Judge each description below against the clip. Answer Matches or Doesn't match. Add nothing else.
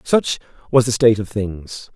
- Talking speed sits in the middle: Matches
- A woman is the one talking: Doesn't match